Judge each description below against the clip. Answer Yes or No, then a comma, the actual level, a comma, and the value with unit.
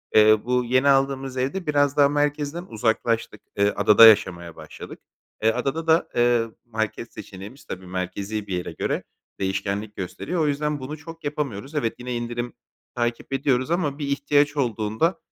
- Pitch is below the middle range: Yes, low, 125 Hz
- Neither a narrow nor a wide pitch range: Yes, average, 4.9 semitones